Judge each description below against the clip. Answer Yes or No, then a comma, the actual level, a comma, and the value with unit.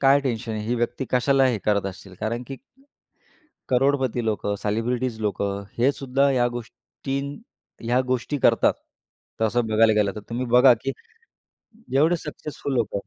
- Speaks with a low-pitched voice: Yes, low, 120 Hz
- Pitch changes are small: No, average, 3.5 semitones